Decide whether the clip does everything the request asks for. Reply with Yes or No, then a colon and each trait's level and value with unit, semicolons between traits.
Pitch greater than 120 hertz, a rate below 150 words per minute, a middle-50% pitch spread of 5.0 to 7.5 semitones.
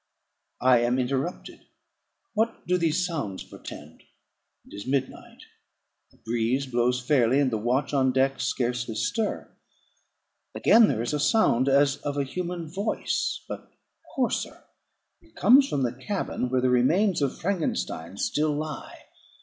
Yes: low, 135 Hz; average, 140 wpm; wide, 5.5 semitones